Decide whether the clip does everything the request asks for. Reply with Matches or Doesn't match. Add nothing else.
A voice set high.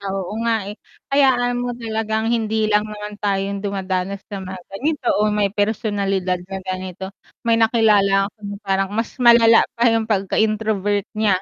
Matches